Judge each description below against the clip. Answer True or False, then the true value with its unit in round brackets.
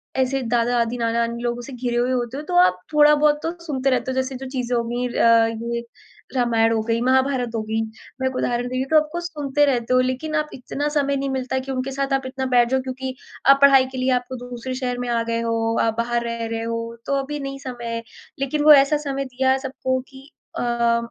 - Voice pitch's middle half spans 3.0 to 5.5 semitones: False (2.4 semitones)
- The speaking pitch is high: True (255 Hz)